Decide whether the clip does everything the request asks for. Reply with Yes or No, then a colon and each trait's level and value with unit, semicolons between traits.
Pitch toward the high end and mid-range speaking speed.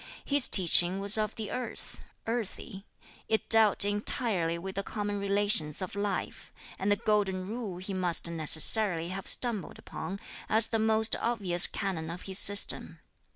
Yes: high, 200 Hz; average, 155 wpm